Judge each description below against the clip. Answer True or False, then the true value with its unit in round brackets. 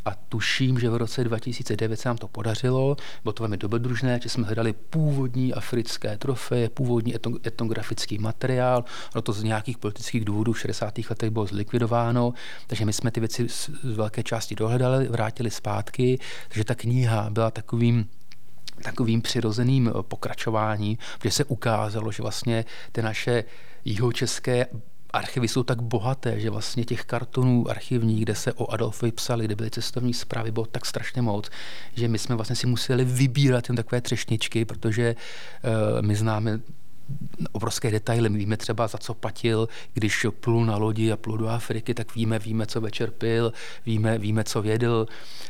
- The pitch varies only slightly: True (1.8 semitones)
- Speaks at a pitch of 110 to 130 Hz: True (115 Hz)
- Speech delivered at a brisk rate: False (160 wpm)